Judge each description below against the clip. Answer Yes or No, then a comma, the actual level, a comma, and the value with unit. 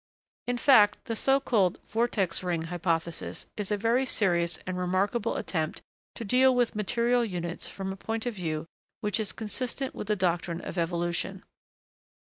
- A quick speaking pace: No, average, 160 wpm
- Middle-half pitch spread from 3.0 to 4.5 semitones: No, average, 5.0 semitones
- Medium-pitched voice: No, high, 200 Hz